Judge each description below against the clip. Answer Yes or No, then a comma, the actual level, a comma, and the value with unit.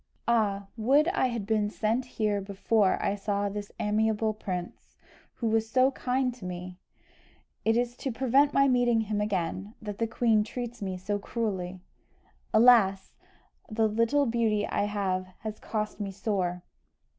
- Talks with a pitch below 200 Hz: No, high, 215 Hz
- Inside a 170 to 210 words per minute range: No, average, 155 wpm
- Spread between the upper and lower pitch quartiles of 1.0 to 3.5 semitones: Yes, average, 2.8 semitones